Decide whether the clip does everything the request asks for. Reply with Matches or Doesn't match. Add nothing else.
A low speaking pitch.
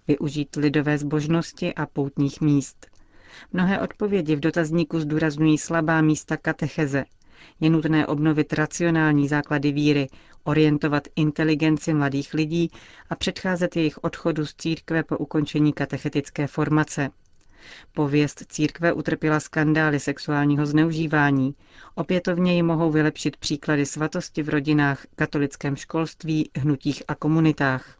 Doesn't match